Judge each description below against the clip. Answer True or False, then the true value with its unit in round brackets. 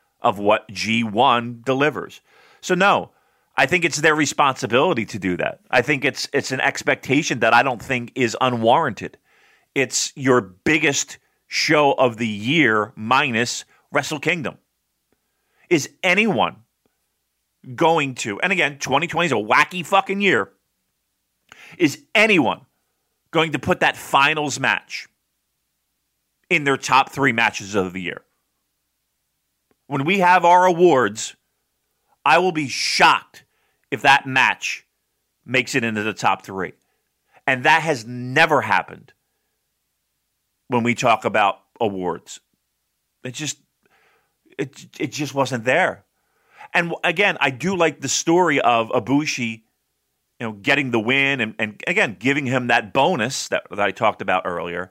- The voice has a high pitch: False (135 Hz)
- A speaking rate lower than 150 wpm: True (140 wpm)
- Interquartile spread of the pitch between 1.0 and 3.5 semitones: False (4.4 semitones)